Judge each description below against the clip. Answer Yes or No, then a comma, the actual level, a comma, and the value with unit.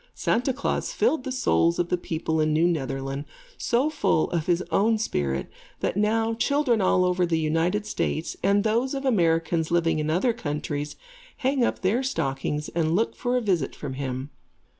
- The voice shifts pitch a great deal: Yes, wide, 6.5 semitones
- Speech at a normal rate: Yes, average, 180 wpm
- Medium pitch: Yes, medium, 175 Hz